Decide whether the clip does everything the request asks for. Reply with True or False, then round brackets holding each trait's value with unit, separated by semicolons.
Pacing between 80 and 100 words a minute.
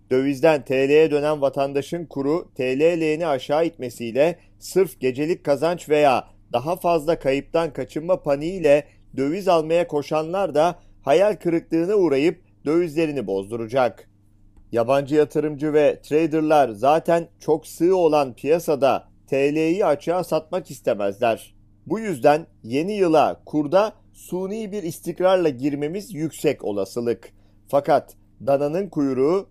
False (110 wpm)